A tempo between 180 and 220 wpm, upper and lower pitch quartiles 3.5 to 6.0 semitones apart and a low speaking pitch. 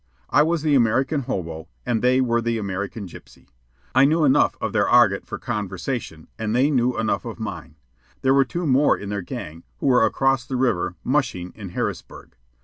Yes: average, 190 wpm; average, 5.2 semitones; low, 120 Hz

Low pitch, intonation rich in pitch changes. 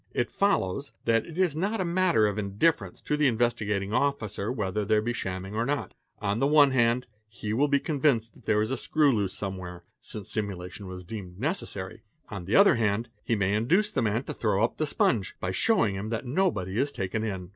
Yes: low, 110 Hz; wide, 6.0 semitones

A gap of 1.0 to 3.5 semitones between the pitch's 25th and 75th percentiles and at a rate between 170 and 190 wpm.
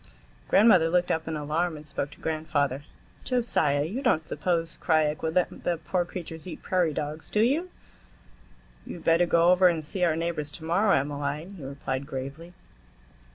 Yes: average, 2.9 semitones; average, 175 wpm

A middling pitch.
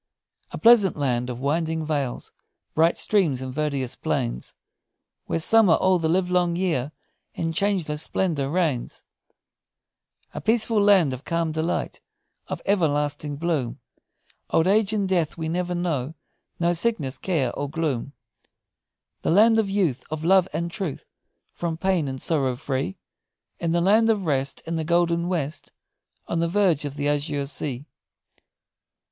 Yes: medium, 165 Hz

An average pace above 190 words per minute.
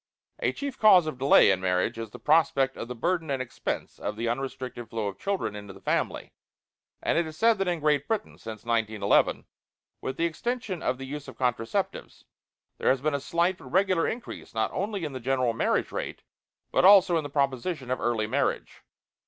Yes: average, 200 wpm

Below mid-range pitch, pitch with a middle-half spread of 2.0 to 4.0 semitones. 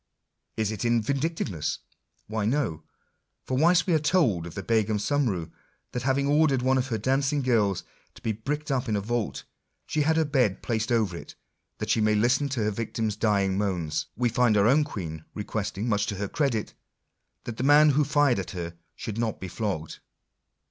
No: low, 115 Hz; average, 5.2 semitones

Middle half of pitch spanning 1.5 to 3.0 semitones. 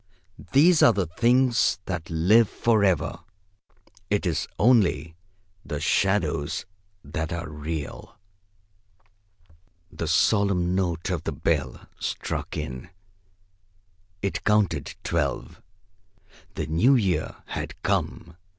No: average, 4.7 semitones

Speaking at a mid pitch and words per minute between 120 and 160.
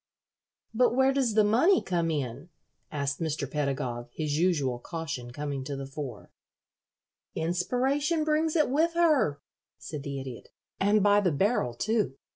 Yes: medium, 165 Hz; average, 145 wpm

